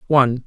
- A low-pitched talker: Yes, low, 130 Hz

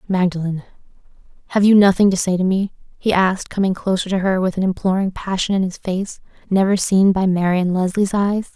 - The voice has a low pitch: No, high, 190 Hz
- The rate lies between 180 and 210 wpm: Yes, average, 190 wpm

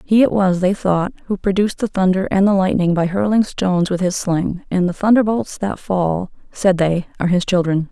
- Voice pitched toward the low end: No, high, 190 Hz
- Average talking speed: No, fast, 210 wpm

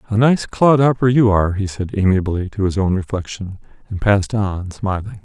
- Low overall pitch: Yes, low, 100 Hz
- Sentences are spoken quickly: No, average, 185 wpm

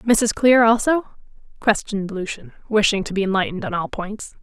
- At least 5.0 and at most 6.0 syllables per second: Yes, 5.5 syllables/s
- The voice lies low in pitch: No, high, 210 Hz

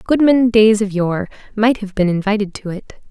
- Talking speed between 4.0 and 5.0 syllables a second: Yes, 4.9 syllables/s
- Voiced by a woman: Yes, female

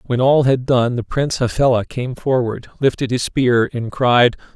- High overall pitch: No, low, 125 Hz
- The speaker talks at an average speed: Yes, average, 185 wpm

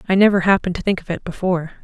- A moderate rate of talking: No, fast, 260 wpm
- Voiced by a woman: Yes, female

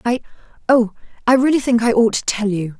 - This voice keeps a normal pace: Yes, average, 170 wpm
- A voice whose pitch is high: Yes, high, 230 Hz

